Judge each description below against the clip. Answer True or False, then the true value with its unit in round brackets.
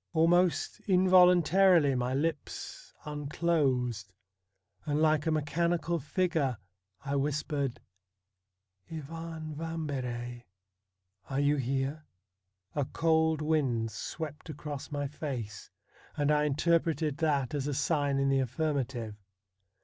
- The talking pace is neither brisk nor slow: False (110 wpm)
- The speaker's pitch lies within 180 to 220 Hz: False (145 Hz)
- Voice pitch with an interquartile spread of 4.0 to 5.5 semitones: False (3.3 semitones)